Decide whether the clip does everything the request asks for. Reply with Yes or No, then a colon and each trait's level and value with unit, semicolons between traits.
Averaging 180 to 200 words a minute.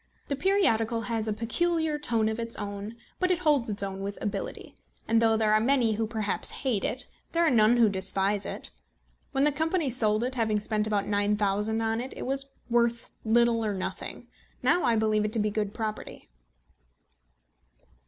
Yes: average, 190 wpm